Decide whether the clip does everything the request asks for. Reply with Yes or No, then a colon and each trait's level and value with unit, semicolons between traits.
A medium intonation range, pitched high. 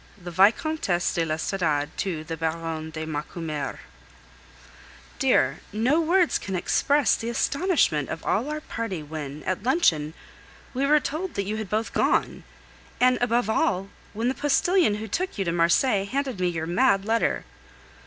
No: wide, 8.1 semitones; high, 200 Hz